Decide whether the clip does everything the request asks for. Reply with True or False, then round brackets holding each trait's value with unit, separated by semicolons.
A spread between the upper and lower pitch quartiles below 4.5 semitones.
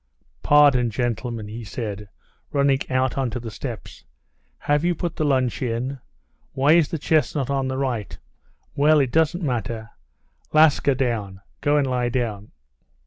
True (3.8 semitones)